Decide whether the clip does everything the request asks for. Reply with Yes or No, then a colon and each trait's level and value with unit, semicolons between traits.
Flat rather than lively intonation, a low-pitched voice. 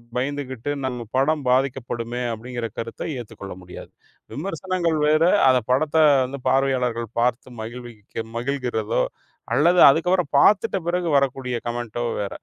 No: average, 3.5 semitones; low, 130 Hz